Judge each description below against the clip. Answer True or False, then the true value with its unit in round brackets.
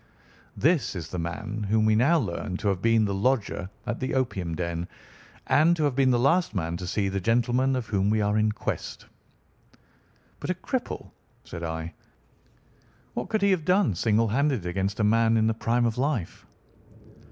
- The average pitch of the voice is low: True (110 Hz)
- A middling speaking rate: True (185 wpm)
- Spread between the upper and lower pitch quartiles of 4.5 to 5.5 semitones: True (5.0 semitones)